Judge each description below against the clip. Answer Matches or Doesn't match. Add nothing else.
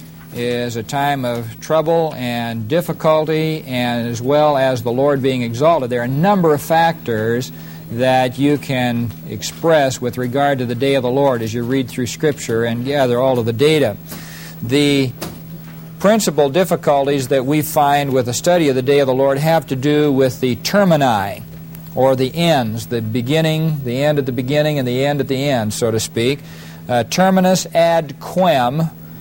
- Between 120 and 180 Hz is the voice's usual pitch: Matches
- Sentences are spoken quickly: Doesn't match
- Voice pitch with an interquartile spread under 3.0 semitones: Doesn't match